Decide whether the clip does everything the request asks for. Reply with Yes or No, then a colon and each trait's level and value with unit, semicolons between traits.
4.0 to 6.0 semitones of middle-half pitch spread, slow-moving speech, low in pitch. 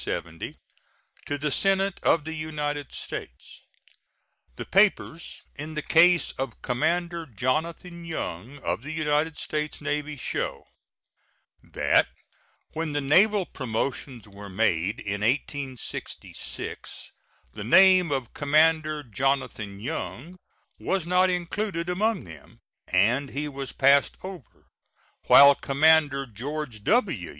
No: average, 4.7 semitones; slow, 110 wpm; medium, 150 Hz